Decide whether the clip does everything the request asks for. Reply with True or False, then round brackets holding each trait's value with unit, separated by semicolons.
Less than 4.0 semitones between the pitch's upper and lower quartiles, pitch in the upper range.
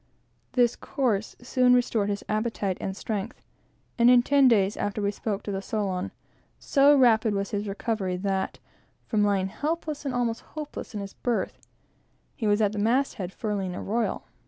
True (3.6 semitones; 215 Hz)